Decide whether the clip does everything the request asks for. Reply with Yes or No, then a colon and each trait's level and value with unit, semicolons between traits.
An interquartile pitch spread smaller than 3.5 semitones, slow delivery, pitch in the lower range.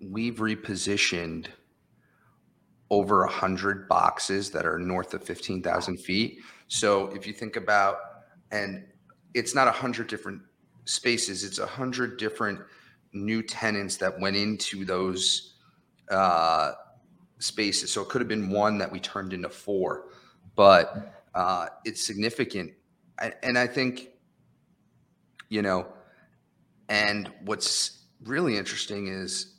Yes: average, 2.8 semitones; slow, 125 wpm; low, 100 Hz